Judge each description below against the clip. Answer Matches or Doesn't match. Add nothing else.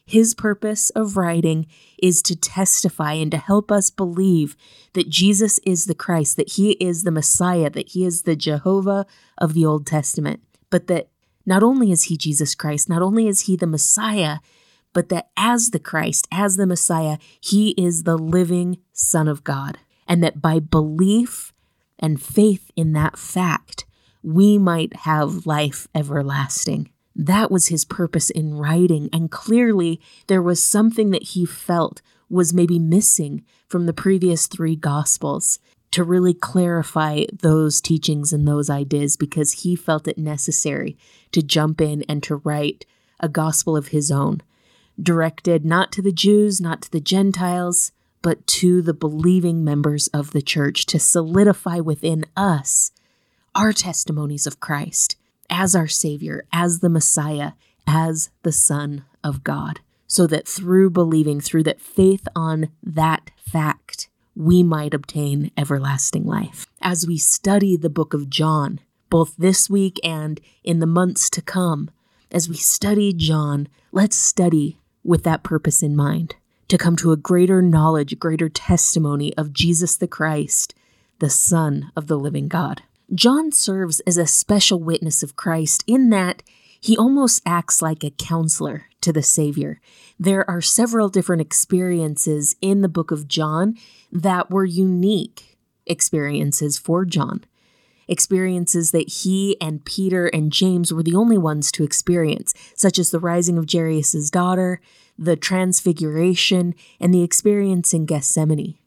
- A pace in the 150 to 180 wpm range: Matches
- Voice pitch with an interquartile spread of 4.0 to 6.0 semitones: Doesn't match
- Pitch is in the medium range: Matches